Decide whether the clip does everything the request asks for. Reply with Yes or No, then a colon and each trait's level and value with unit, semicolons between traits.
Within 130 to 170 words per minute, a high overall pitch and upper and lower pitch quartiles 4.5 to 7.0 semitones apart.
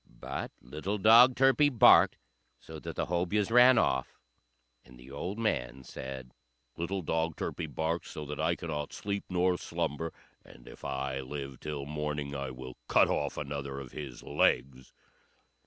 No: average, 155 wpm; very low, 75 Hz; average, 5.0 semitones